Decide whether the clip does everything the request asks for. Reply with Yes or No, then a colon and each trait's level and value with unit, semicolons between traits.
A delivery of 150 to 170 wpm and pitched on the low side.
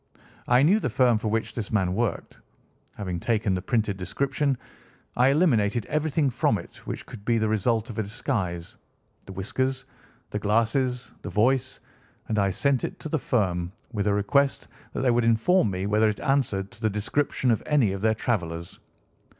No: average, 180 wpm; low, 110 Hz